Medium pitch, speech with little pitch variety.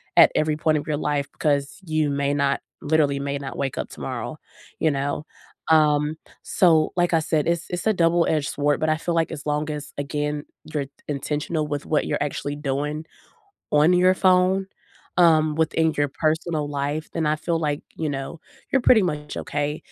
Yes: medium, 150 Hz; narrow, 1.8 semitones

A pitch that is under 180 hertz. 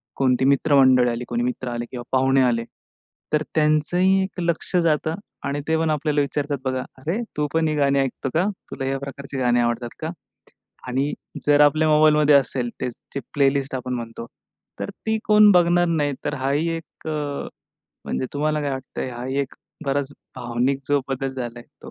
Yes: medium, 140 Hz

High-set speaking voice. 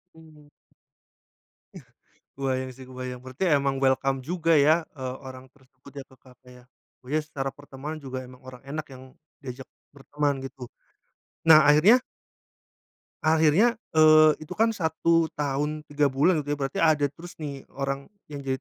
No: medium, 145 Hz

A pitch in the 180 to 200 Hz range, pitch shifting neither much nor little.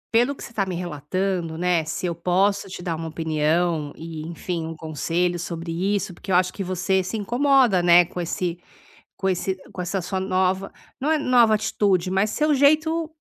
Yes: medium, 185 Hz; average, 3.0 semitones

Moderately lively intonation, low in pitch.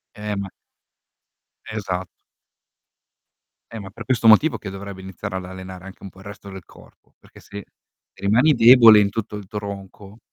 No: narrow, 2.0 semitones; low, 100 Hz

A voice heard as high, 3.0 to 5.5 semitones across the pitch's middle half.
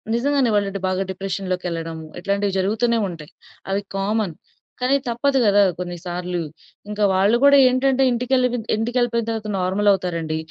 Yes: high, 205 Hz; average, 4.6 semitones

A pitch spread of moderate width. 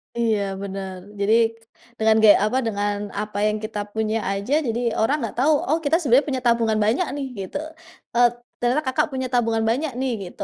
Yes: average, 3.5 semitones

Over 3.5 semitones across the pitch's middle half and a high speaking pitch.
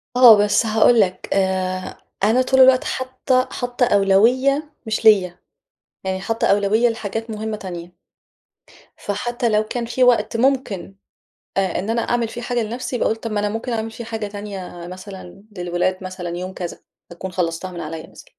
Yes: average, 4.1 semitones; high, 210 Hz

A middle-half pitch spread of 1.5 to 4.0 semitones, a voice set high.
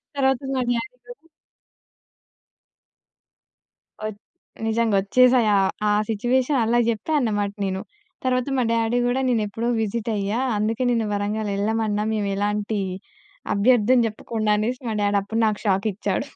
Yes: average, 2.8 semitones; high, 220 Hz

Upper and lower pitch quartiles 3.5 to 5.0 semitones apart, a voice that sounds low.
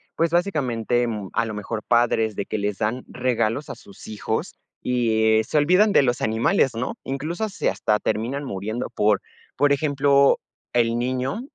Yes: average, 4.1 semitones; low, 120 Hz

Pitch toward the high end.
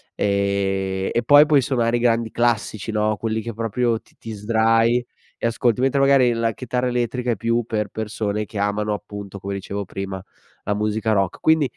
No: low, 110 Hz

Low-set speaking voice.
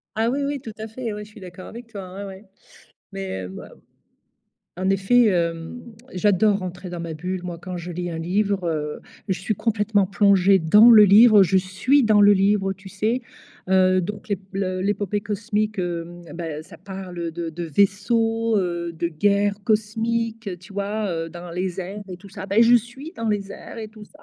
No: high, 195 Hz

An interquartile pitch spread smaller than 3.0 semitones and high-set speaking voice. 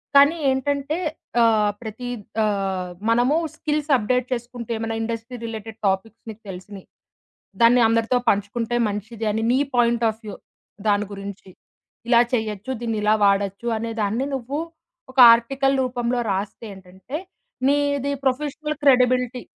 No: average, 3.4 semitones; high, 230 Hz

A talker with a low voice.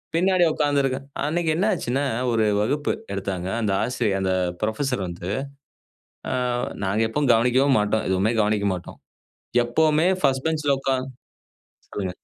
Yes: low, 125 Hz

